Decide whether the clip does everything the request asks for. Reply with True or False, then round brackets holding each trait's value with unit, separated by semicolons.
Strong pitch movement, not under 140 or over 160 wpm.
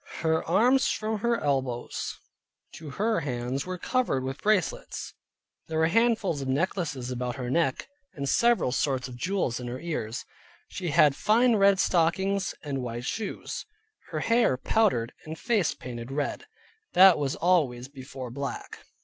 True (7.3 semitones; 150 wpm)